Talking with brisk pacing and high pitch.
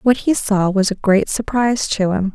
Yes: fast, 230 wpm; high, 210 Hz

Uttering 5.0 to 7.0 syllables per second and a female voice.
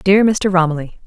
Yes: 5.1 syllables/s; female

